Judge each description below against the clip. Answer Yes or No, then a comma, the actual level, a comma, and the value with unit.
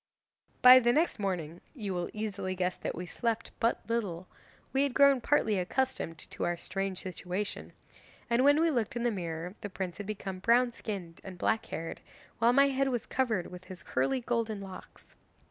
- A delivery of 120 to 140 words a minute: No, average, 185 wpm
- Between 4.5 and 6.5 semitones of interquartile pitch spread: Yes, average, 5.0 semitones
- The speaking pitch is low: No, high, 210 Hz